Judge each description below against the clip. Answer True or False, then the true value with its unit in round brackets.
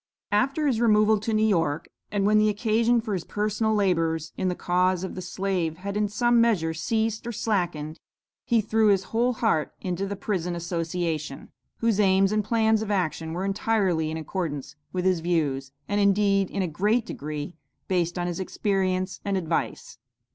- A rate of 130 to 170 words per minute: False (180 wpm)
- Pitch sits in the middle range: False (195 Hz)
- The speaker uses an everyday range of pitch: True (3.8 semitones)